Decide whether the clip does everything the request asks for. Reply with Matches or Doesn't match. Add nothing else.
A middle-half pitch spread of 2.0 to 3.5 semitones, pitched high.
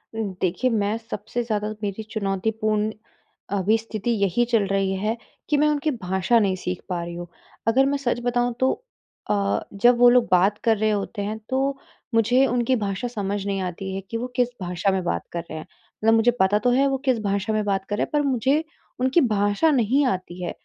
Doesn't match